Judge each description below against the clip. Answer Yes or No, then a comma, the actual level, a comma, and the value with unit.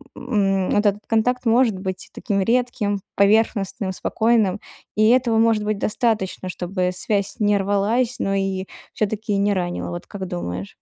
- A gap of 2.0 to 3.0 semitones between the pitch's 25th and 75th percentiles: Yes, average, 2.7 semitones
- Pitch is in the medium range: No, high, 205 Hz